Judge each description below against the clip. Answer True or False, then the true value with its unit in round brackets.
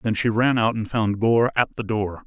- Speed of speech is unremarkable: False (265 wpm)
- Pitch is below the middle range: True (110 Hz)